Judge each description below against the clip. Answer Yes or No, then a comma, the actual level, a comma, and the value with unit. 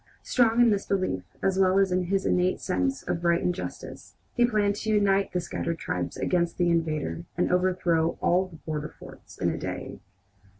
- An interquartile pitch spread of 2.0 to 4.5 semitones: Yes, narrow, 2.6 semitones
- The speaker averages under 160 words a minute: No, average, 195 wpm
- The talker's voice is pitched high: No, medium, 180 Hz